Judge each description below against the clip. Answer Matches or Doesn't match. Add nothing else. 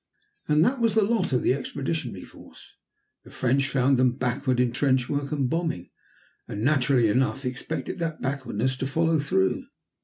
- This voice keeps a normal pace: Matches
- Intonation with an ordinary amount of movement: Matches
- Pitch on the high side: Doesn't match